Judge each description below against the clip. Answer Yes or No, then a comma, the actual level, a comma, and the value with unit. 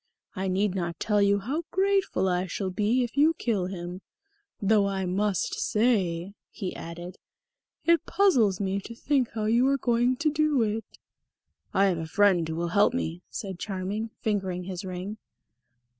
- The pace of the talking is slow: No, average, 170 wpm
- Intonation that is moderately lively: Yes, average, 4.2 semitones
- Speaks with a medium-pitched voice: No, high, 200 Hz